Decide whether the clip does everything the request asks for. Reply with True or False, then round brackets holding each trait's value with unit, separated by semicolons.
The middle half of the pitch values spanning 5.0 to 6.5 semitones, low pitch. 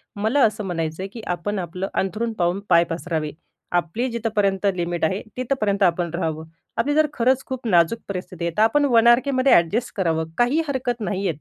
False (5.5 semitones; 200 Hz)